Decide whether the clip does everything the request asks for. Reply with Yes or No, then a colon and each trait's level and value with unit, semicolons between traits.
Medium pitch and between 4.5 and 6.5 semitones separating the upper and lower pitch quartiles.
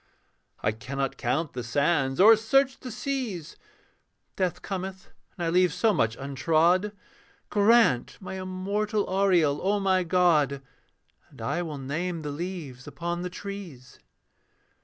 Yes: medium, 175 Hz; wide, 5.6 semitones